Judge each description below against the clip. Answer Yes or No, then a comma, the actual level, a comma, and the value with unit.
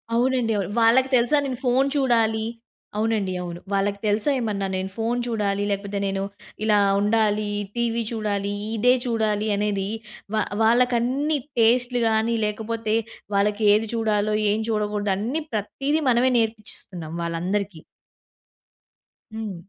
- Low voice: No, high, 220 Hz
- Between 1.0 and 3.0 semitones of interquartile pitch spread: Yes, narrow, 2.5 semitones